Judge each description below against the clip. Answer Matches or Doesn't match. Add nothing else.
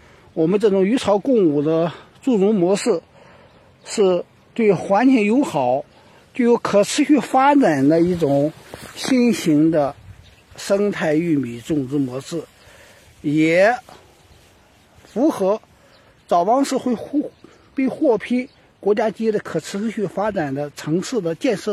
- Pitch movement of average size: Doesn't match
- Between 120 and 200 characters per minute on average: Matches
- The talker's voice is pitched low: Doesn't match